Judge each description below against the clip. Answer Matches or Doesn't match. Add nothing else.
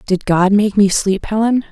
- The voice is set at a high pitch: Matches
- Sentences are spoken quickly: Matches